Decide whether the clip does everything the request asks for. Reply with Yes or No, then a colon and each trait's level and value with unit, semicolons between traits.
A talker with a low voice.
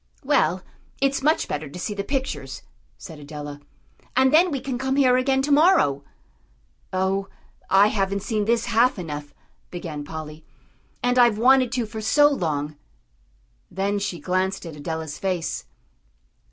No: high, 200 Hz